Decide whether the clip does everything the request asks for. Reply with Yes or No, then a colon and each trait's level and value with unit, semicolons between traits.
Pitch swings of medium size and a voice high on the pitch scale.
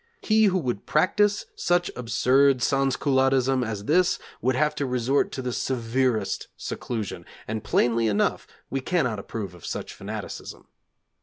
No: average, 3.7 semitones; low, 130 Hz